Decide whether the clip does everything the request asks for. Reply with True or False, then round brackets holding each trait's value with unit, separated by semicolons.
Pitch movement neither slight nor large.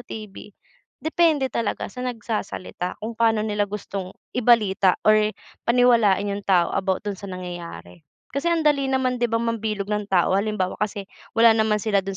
True (3.0 semitones)